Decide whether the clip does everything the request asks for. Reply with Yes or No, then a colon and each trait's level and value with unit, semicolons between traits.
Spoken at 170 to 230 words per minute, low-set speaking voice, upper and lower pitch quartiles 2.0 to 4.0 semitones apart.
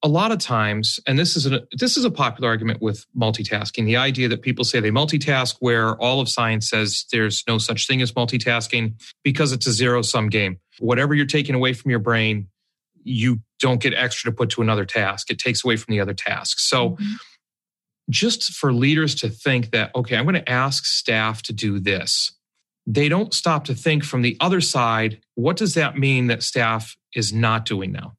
Yes: fast, 205 wpm; low, 120 Hz; average, 3.7 semitones